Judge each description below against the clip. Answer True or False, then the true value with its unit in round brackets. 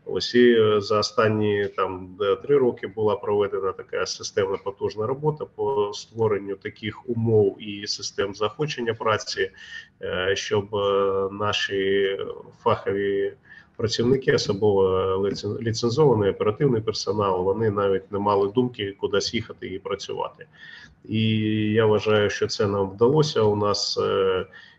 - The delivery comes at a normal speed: True (115 wpm)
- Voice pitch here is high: False (110 Hz)